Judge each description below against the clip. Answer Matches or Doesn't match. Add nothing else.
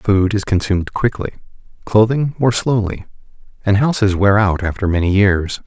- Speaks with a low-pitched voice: Matches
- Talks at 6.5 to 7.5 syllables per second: Doesn't match